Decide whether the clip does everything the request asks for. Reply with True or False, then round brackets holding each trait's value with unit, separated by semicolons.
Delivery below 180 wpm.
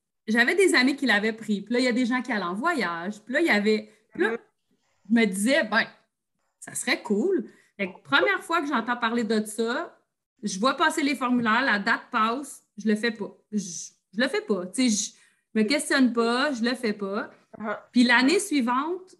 False (210 wpm)